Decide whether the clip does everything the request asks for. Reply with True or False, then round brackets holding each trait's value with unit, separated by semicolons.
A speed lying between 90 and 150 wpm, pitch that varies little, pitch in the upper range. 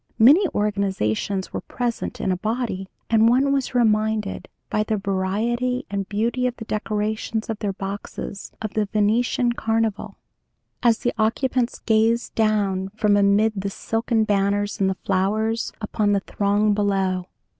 True (145 wpm; 2.3 semitones; 215 Hz)